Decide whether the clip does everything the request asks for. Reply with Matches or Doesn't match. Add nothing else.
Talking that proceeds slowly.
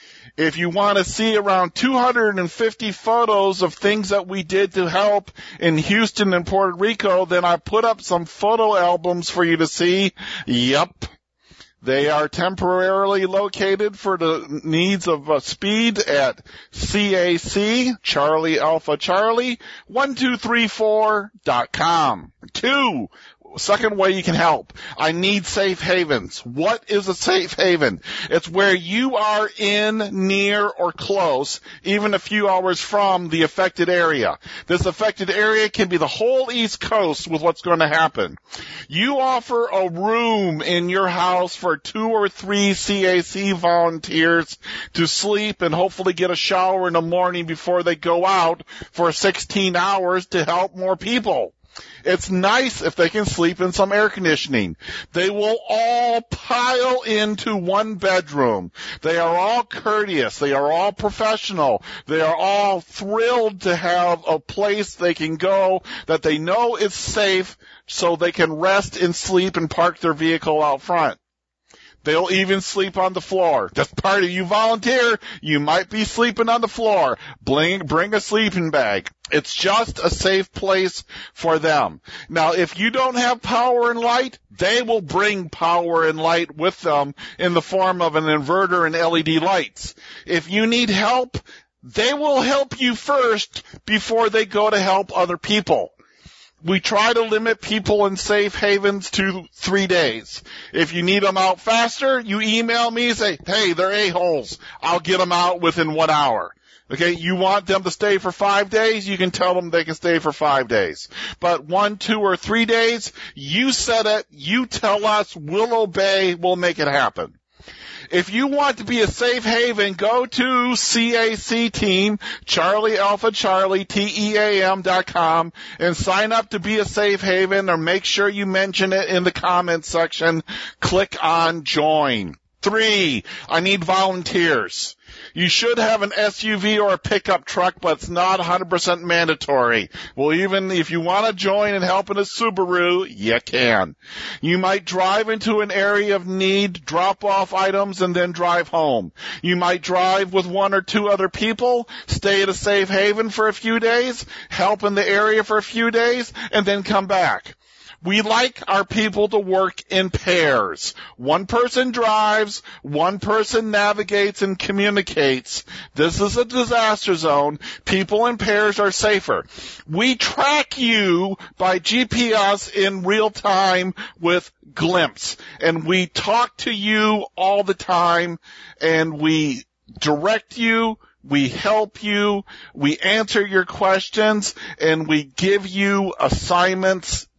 Doesn't match